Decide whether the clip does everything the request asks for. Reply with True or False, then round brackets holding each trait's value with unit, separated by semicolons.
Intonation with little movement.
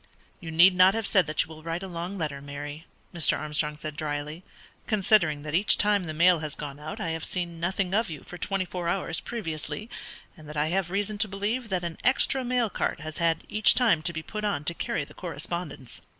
False (4.2 semitones)